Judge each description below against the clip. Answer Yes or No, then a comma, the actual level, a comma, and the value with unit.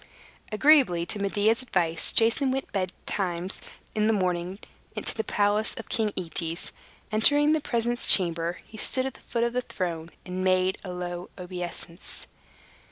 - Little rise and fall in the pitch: No, average, 4.4 semitones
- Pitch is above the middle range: Yes, high, 195 Hz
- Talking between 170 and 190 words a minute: No, average, 155 wpm